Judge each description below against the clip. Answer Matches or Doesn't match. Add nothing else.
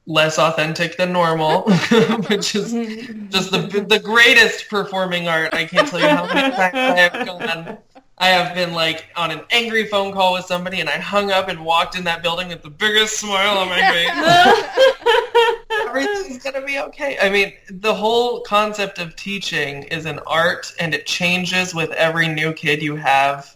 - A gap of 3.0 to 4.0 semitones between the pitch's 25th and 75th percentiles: Doesn't match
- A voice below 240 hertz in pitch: Matches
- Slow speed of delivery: Doesn't match